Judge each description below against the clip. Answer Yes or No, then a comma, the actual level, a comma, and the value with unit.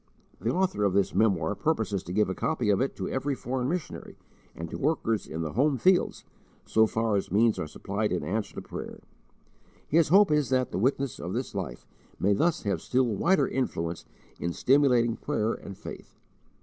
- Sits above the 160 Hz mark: No, low, 115 Hz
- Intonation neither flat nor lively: No, wide, 6.0 semitones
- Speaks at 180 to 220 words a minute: Yes, average, 190 wpm